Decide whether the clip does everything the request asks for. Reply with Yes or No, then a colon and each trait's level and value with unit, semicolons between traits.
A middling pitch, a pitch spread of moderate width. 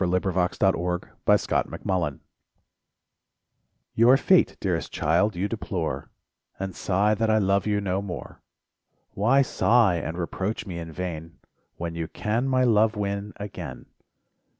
No: low, 100 Hz; average, 3.4 semitones